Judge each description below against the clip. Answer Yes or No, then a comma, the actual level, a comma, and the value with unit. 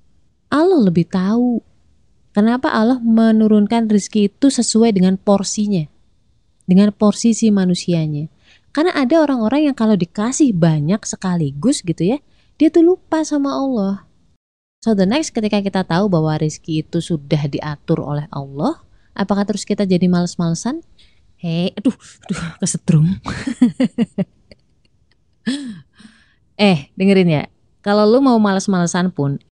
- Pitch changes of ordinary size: Yes, average, 5.0 semitones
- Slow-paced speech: No, average, 120 wpm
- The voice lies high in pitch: Yes, high, 205 Hz